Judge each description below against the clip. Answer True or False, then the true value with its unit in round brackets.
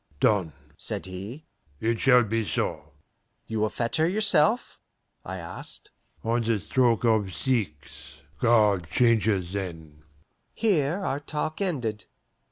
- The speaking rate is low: True (125 wpm)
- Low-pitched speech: True (115 Hz)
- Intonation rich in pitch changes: True (6.0 semitones)